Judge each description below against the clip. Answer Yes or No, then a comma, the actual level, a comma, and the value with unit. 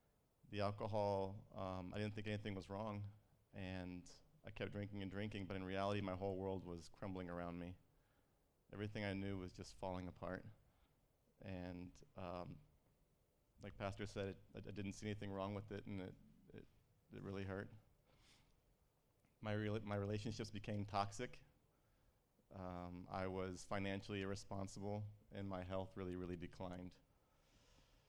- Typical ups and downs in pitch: No, narrow, 1.9 semitones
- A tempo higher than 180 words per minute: No, average, 145 wpm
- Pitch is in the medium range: No, low, 100 Hz